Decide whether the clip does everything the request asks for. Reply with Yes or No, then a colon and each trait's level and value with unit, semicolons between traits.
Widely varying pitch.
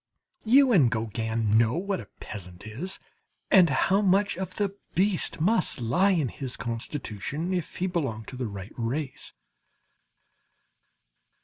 Yes: wide, 8.8 semitones